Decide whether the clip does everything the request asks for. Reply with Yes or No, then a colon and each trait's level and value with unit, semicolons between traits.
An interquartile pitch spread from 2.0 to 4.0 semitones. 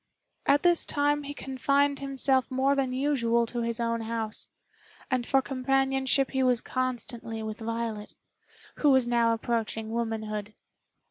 Yes: average, 2.8 semitones